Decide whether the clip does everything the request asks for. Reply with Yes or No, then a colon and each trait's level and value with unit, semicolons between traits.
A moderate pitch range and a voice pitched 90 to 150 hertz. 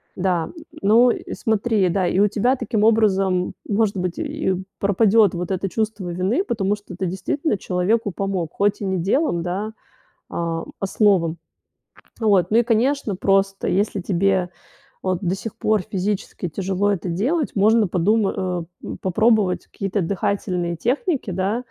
No: average, 3.1 semitones; high, 195 Hz